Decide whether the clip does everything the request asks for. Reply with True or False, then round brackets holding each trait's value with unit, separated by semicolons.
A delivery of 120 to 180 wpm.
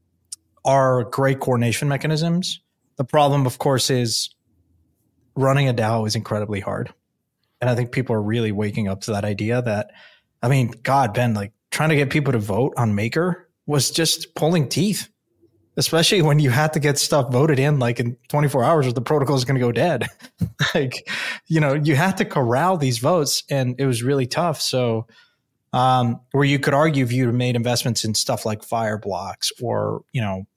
False (190 wpm)